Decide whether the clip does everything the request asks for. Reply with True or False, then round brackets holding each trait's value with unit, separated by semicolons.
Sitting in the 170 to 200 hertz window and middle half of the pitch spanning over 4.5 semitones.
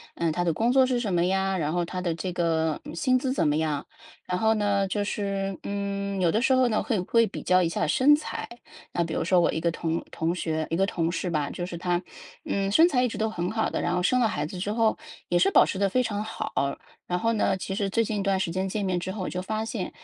False (190 Hz; 3.8 semitones)